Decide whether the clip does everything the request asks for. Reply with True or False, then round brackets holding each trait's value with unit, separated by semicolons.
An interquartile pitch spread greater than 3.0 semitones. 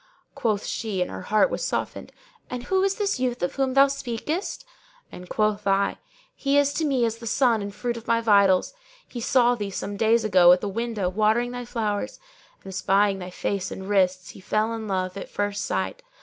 True (3.7 semitones)